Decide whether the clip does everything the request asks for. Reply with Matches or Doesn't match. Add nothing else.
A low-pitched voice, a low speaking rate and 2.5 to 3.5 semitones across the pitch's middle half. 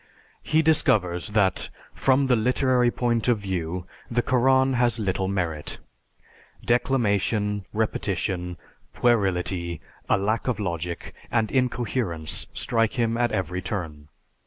Doesn't match